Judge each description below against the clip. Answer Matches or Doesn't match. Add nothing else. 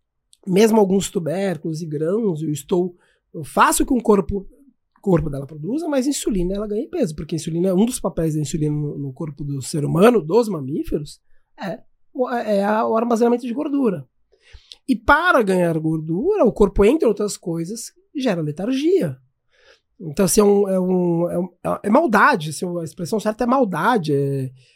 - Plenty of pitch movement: Matches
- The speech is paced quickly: Doesn't match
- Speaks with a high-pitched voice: Matches